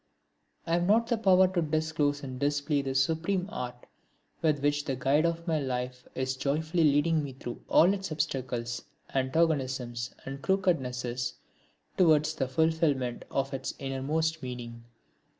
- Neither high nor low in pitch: Yes, medium, 145 Hz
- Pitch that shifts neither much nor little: Yes, average, 3.7 semitones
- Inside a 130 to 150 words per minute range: Yes, average, 145 wpm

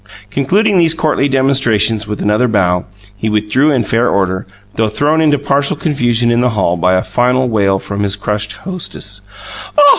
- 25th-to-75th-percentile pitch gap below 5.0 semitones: No, wide, 5.4 semitones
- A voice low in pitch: Yes, low, 120 Hz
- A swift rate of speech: No, average, 175 wpm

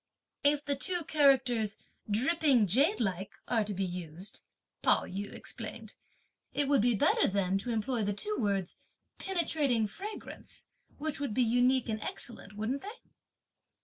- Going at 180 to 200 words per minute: No, average, 145 wpm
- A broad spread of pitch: Yes, wide, 5.8 semitones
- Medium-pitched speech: No, high, 240 Hz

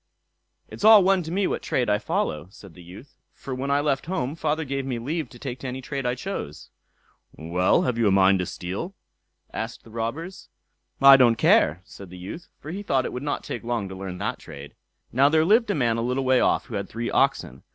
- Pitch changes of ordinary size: No, wide, 6.8 semitones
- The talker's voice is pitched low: Yes, low, 125 Hz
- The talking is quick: Yes, fast, 235 wpm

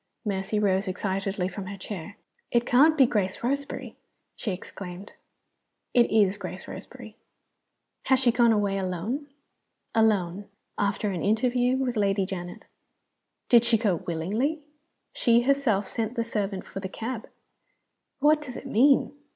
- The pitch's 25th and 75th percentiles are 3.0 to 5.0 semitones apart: Yes, average, 4.2 semitones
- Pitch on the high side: Yes, high, 210 Hz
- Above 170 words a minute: No, average, 140 wpm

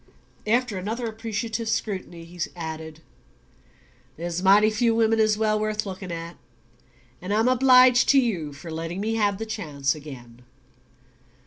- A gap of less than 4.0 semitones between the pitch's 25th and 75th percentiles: No, average, 5.1 semitones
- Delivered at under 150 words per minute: Yes, average, 140 wpm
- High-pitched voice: Yes, high, 205 Hz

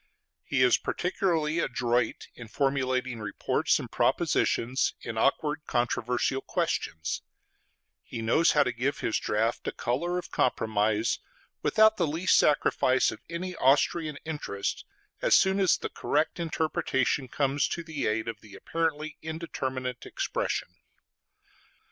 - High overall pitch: No, low, 135 Hz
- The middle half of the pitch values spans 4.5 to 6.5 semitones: Yes, average, 5.1 semitones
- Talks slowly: Yes, slow, 130 wpm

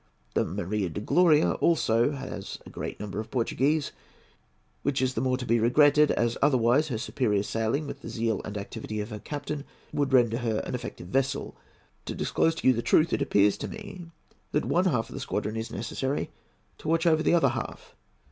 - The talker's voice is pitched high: No, low, 130 Hz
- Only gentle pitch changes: No, average, 5.0 semitones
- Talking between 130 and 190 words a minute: No, average, 200 wpm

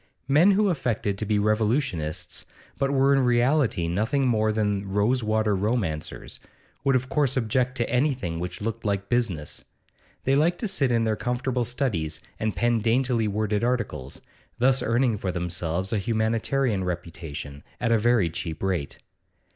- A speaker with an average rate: Yes, average, 155 wpm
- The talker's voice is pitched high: No, low, 110 Hz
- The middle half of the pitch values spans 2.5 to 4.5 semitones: No, average, 4.9 semitones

